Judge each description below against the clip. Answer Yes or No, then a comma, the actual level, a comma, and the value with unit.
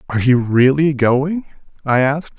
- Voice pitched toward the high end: No, low, 135 Hz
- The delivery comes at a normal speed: Yes, average, 150 wpm